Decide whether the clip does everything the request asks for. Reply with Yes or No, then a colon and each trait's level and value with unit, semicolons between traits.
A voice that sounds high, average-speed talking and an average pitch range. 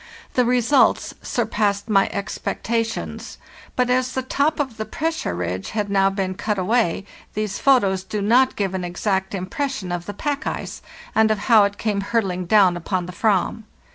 Yes: high, 205 Hz; average, 170 wpm; average, 3.8 semitones